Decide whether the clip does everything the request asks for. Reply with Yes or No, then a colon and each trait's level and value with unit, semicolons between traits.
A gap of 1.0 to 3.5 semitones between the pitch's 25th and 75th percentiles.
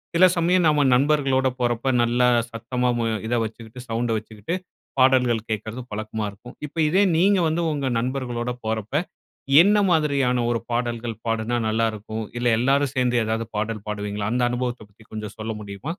Yes: average, 3.2 semitones